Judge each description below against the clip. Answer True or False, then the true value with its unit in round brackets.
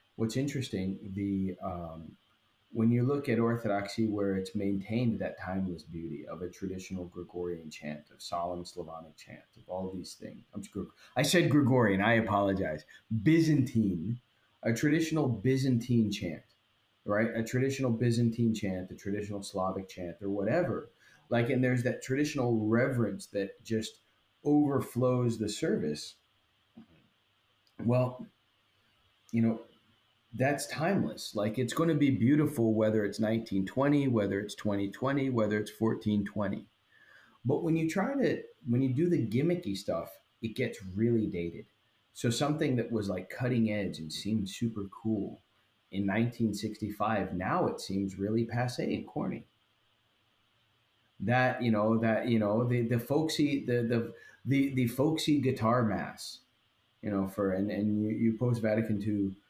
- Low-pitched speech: True (110 Hz)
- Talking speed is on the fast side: False (150 wpm)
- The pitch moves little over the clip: False (3.8 semitones)